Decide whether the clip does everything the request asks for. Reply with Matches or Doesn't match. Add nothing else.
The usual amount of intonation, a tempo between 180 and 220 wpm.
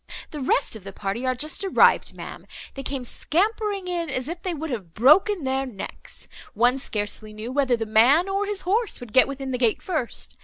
Doesn't match